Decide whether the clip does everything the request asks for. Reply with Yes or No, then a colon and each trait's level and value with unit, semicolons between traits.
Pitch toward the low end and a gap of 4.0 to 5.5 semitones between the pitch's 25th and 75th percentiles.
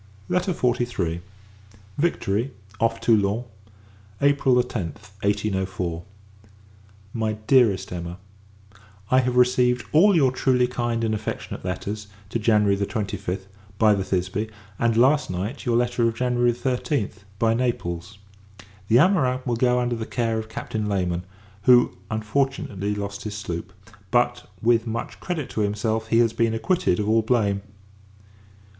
No: low, 115 Hz; average, 3.4 semitones